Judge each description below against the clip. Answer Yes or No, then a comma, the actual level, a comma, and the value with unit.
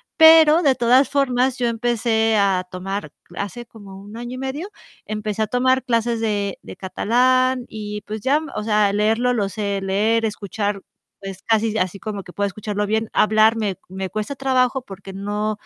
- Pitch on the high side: Yes, high, 215 Hz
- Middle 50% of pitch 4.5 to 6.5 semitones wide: No, average, 3.5 semitones